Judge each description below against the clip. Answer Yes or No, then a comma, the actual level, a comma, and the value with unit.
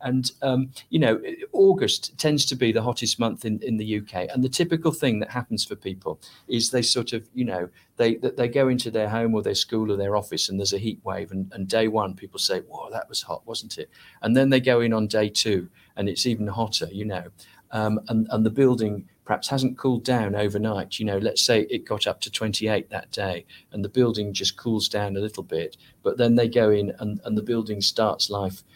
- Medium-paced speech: No, fast, 235 wpm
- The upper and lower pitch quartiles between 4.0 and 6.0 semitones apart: No, average, 3.4 semitones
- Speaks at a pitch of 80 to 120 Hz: Yes, low, 110 Hz